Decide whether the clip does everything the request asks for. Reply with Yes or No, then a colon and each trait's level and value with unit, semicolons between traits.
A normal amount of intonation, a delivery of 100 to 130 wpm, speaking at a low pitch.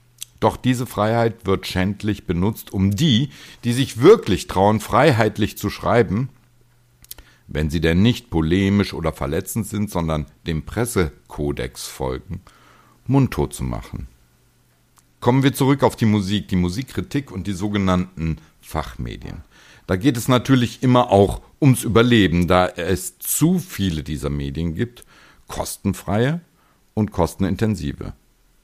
No: wide, 6.5 semitones; slow, 125 wpm; low, 100 Hz